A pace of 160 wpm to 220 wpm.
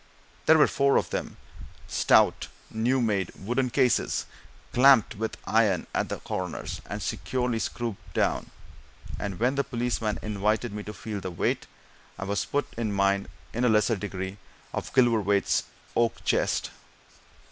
No: average, 145 wpm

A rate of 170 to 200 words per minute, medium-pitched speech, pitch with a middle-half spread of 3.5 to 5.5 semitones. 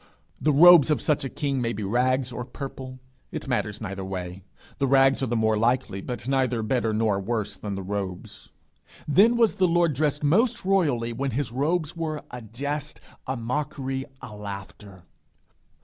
No: average, 175 wpm; low, 130 Hz; average, 5.2 semitones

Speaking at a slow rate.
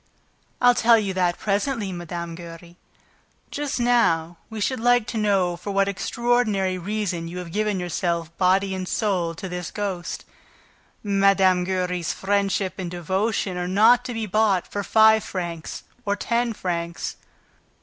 No: average, 150 wpm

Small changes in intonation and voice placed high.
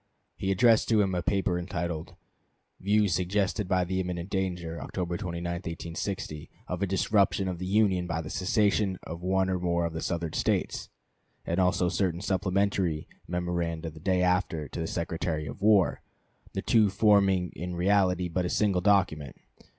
No: narrow, 2.1 semitones; very low, 90 Hz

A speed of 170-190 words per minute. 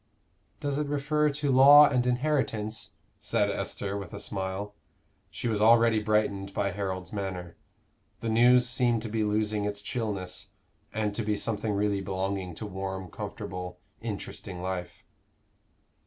No: average, 140 wpm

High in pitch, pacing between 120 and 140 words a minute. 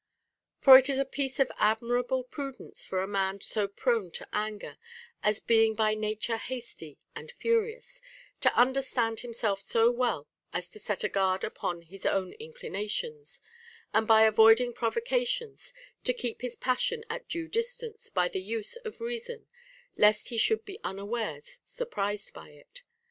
No: high, 235 Hz; average, 160 wpm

